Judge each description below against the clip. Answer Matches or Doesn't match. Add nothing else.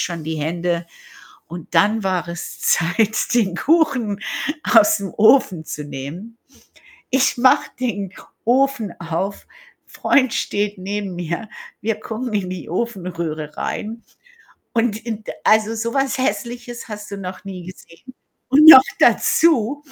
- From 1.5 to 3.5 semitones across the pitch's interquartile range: Doesn't match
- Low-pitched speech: Doesn't match